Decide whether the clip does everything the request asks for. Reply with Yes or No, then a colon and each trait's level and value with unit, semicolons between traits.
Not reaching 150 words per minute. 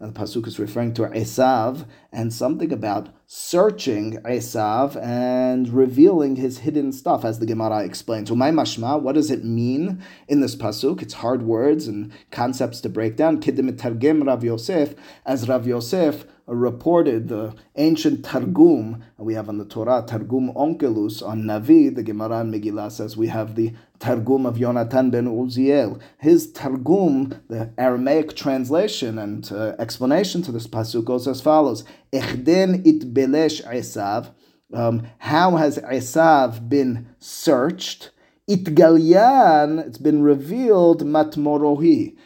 Yes: average, 140 wpm